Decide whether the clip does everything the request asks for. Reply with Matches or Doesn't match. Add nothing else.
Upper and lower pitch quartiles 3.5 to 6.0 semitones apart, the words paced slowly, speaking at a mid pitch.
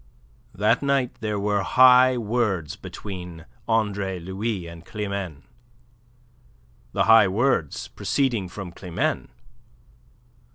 Doesn't match